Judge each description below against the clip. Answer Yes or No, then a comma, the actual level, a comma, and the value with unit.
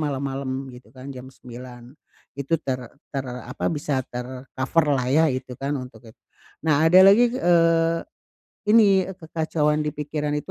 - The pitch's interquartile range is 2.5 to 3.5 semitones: No, average, 4.0 semitones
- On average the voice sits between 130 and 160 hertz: Yes, medium, 140 Hz